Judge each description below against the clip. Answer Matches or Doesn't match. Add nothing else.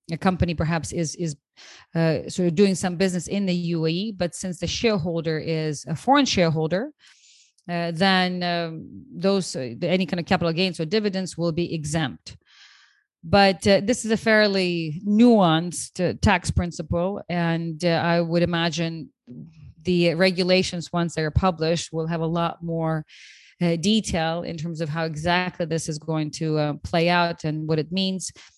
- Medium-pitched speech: Matches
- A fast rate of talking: Doesn't match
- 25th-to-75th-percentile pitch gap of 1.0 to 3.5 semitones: Matches